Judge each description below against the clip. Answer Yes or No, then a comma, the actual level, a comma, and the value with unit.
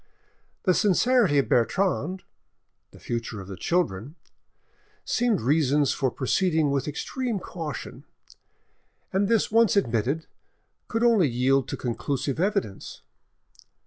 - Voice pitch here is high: No, medium, 155 Hz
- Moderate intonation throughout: No, wide, 7.3 semitones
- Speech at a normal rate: No, slow, 115 wpm